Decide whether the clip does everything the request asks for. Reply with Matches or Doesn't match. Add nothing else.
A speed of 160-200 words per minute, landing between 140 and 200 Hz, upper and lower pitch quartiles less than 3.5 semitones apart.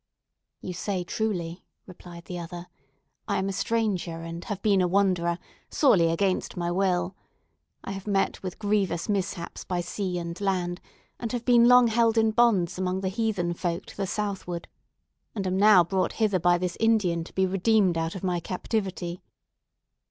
Matches